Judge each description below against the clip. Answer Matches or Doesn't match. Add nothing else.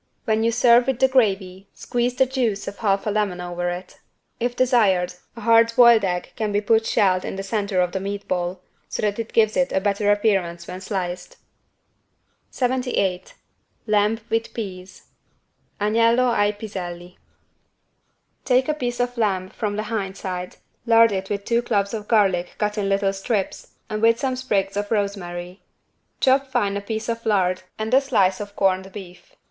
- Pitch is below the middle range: Doesn't match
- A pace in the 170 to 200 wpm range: Matches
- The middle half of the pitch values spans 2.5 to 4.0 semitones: Matches